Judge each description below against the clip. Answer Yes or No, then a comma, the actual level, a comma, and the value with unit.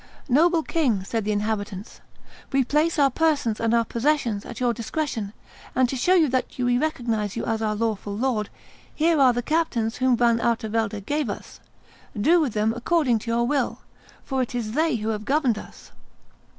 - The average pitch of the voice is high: Yes, high, 240 Hz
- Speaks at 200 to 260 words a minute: No, average, 185 wpm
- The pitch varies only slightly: No, average, 4.6 semitones